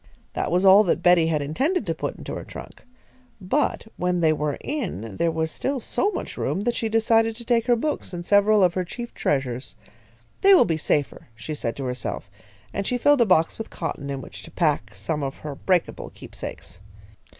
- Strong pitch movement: Yes, wide, 7.2 semitones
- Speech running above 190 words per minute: Yes, fast, 205 wpm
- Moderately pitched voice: Yes, medium, 180 Hz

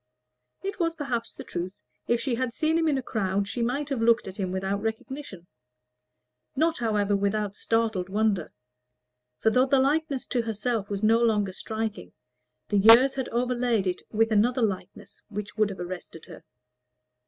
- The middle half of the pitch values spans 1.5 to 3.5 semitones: No, average, 4.0 semitones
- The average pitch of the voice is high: Yes, high, 225 Hz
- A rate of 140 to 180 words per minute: Yes, average, 170 wpm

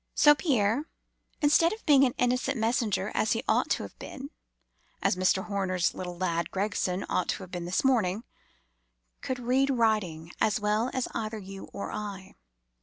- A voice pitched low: No, high, 210 Hz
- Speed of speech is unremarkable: Yes, average, 160 wpm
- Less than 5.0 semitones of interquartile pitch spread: No, average, 5.3 semitones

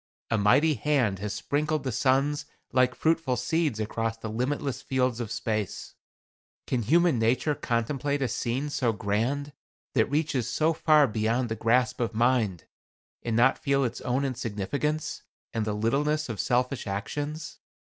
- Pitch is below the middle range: Yes, low, 125 Hz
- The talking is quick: No, average, 150 wpm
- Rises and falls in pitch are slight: No, average, 4.2 semitones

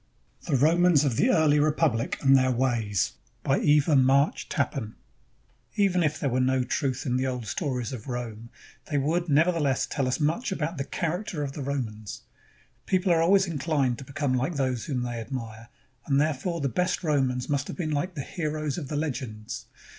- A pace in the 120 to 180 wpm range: No, average, 190 wpm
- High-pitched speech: No, medium, 140 Hz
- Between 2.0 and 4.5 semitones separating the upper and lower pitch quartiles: Yes, average, 3.7 semitones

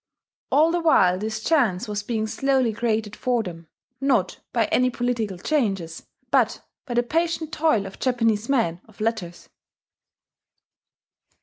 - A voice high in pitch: Yes, high, 225 Hz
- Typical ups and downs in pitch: Yes, average, 4.3 semitones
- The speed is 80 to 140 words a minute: Yes, slow, 135 wpm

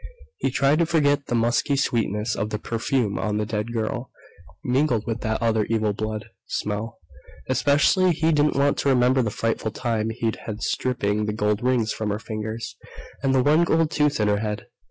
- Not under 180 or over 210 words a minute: Yes, average, 190 wpm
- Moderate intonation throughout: Yes, average, 4.2 semitones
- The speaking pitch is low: Yes, low, 115 Hz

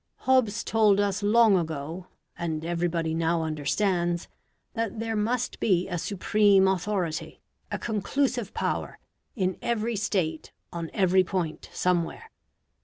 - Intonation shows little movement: No, average, 4.0 semitones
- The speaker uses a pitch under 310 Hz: Yes, high, 190 Hz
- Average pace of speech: No, slow, 120 wpm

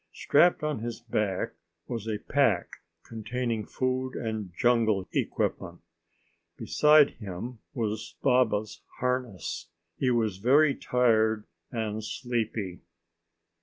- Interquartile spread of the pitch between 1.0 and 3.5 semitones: Yes, average, 2.9 semitones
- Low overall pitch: Yes, low, 115 Hz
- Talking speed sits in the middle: No, slow, 100 wpm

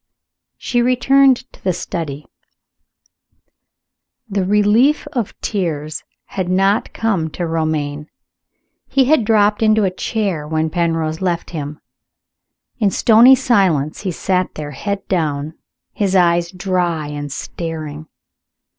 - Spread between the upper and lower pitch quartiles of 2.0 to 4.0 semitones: No, average, 5.0 semitones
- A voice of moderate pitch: Yes, medium, 180 Hz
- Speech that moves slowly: Yes, slow, 120 wpm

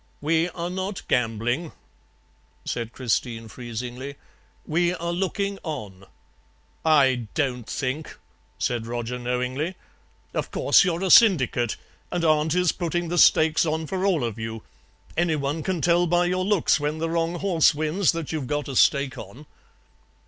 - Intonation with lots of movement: Yes, wide, 5.8 semitones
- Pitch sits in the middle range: Yes, medium, 155 Hz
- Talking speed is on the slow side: No, average, 150 wpm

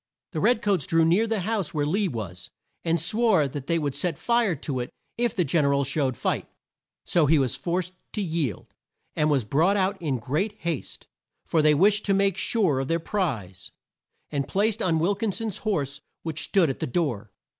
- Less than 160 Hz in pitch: No, medium, 165 Hz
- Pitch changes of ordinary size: No, wide, 6.0 semitones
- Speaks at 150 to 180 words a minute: No, fast, 205 wpm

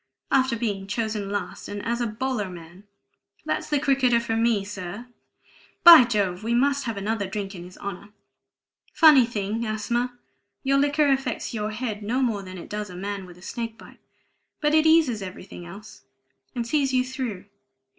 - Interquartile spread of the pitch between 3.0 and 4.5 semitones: Yes, average, 4.2 semitones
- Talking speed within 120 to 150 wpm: No, average, 175 wpm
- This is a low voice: No, high, 225 Hz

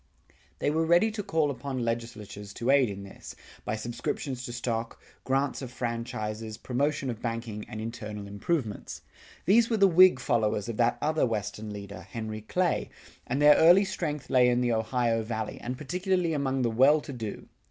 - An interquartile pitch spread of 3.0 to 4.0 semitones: No, average, 5.0 semitones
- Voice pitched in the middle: No, low, 120 Hz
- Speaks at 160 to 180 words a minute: Yes, average, 175 wpm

